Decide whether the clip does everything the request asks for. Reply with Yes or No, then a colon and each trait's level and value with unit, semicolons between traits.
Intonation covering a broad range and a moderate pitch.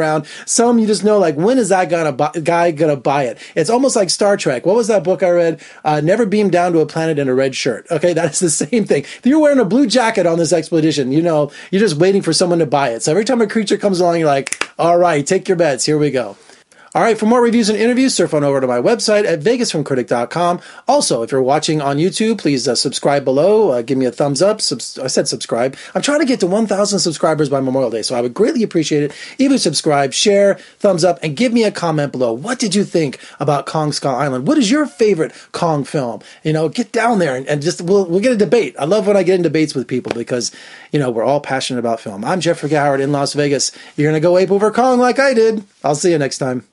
Yes: wide, 6.2 semitones; medium, 170 Hz